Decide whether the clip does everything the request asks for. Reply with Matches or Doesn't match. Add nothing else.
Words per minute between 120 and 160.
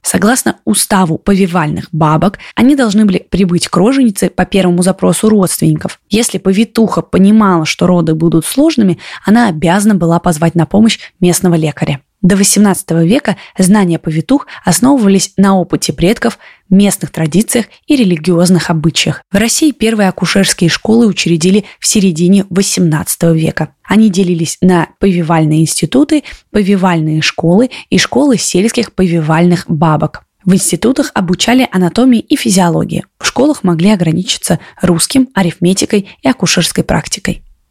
Matches